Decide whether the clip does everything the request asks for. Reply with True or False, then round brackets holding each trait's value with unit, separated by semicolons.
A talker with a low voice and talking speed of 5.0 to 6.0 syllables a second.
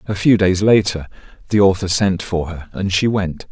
False (95 Hz; 4.8 syllables/s)